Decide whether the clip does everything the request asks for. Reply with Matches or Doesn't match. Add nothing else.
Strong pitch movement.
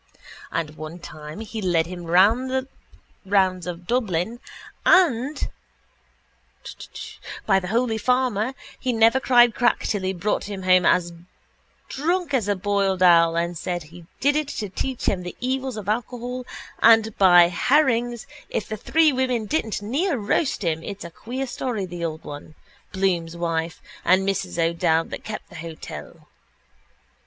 Matches